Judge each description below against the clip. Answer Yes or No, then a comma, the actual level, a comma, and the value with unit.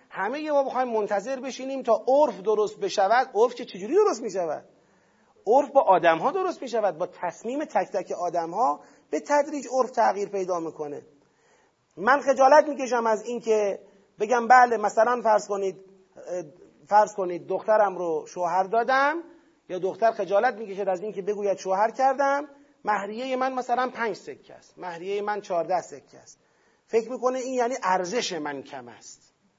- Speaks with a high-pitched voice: Yes, high, 220 Hz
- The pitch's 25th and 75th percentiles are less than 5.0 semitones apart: No, average, 5.3 semitones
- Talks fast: Yes, fast, 160 wpm